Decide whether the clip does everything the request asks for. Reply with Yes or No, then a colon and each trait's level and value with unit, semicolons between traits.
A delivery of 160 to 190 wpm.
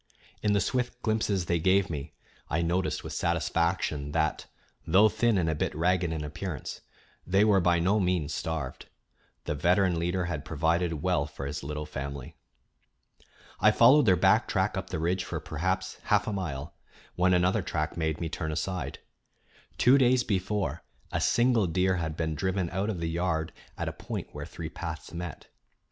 Yes: average, 175 wpm